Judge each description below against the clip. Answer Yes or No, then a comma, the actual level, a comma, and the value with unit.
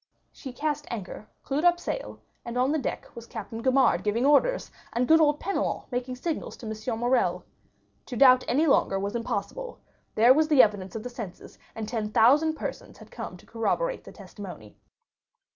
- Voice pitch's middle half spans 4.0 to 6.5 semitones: Yes, average, 5.0 semitones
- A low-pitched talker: No, very high, 250 Hz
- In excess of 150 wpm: Yes, average, 180 wpm